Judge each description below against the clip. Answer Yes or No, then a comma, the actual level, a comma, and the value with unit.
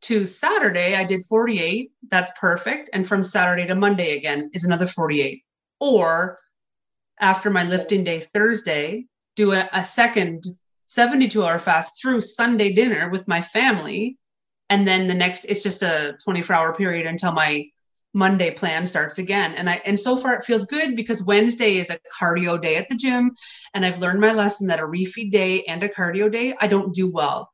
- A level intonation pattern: No, average, 3.5 semitones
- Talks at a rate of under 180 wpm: No, average, 185 wpm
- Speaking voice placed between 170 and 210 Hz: Yes, high, 190 Hz